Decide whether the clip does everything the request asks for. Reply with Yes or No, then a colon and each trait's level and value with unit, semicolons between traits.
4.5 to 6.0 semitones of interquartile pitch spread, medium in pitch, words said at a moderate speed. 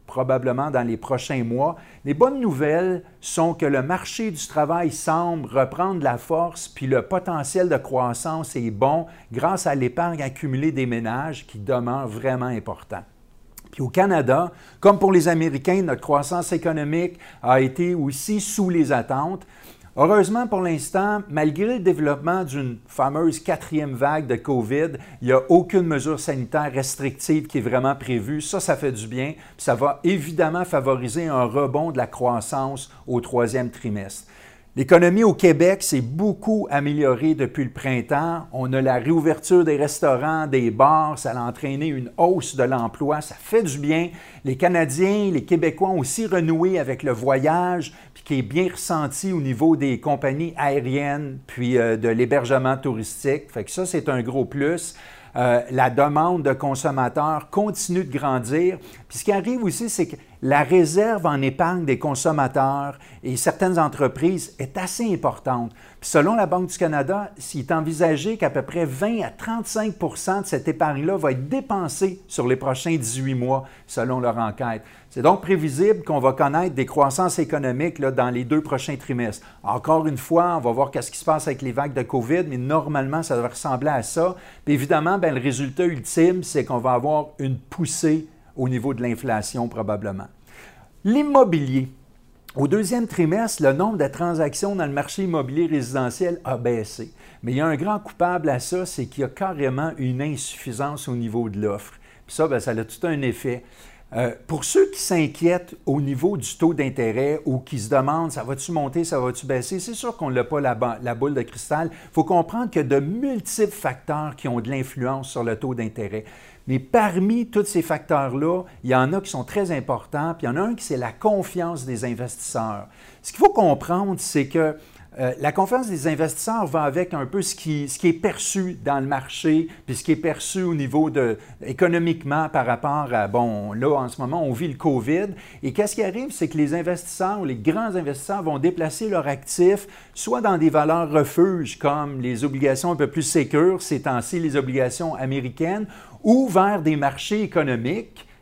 Yes: average, 4.9 semitones; medium, 150 Hz; average, 185 wpm